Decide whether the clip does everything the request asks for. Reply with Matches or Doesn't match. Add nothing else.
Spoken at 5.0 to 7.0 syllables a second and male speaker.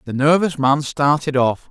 Doesn't match